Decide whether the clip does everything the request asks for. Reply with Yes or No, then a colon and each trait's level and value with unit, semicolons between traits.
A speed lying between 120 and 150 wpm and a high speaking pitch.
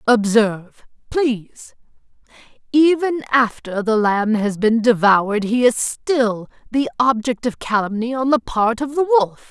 Yes: slow, 135 wpm; high, 235 Hz